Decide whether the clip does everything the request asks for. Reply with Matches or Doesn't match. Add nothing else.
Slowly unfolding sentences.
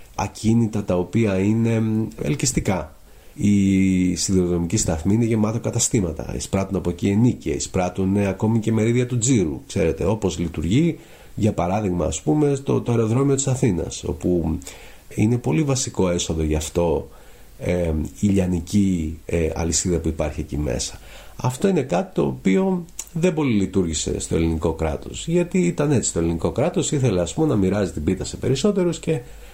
Doesn't match